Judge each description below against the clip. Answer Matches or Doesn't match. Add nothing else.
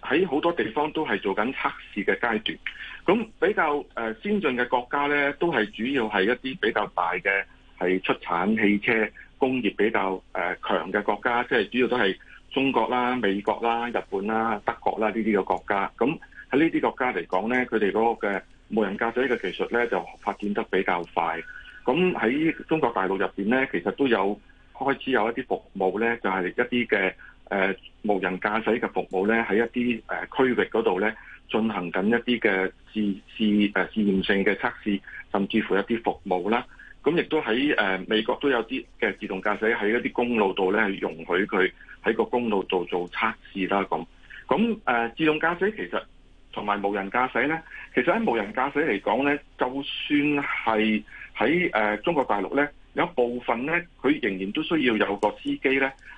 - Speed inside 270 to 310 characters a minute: Matches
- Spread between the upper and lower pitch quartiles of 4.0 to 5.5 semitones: Matches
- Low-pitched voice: Matches